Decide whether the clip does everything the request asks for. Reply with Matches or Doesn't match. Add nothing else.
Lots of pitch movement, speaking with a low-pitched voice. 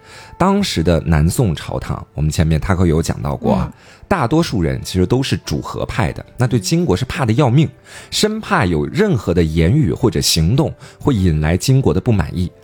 Matches